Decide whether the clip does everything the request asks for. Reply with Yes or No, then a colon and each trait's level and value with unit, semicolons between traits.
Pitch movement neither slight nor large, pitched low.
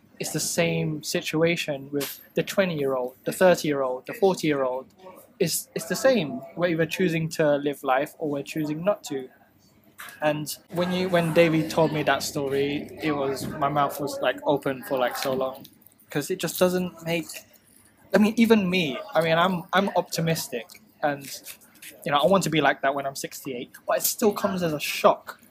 No: average, 4.3 semitones; medium, 160 Hz